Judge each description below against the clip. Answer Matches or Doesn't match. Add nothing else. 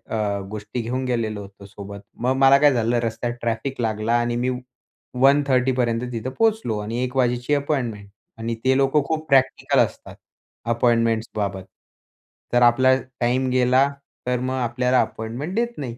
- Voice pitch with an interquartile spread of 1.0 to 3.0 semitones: Matches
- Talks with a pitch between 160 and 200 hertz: Doesn't match